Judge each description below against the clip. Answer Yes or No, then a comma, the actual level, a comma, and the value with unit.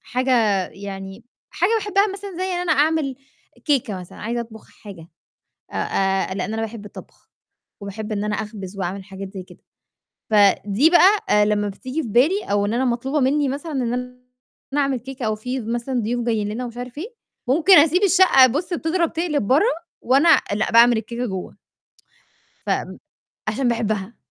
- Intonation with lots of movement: Yes, wide, 6.0 semitones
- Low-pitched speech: No, high, 240 Hz